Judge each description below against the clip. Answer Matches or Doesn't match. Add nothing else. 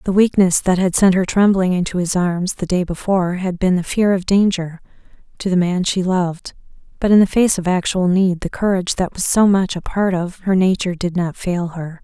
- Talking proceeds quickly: Matches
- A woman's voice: Matches